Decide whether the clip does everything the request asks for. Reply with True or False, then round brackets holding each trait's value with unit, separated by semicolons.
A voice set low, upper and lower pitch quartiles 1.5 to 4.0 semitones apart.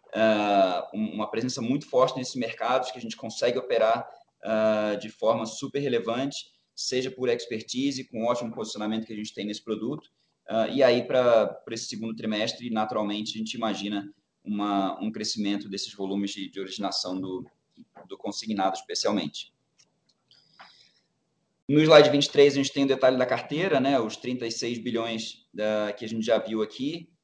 True (110 Hz; 3.6 semitones)